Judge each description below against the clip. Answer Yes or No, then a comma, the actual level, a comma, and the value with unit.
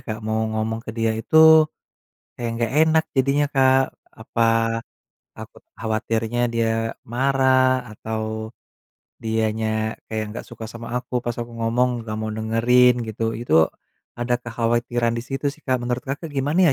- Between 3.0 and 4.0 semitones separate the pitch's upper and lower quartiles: No, narrow, 2.4 semitones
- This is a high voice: No, low, 115 Hz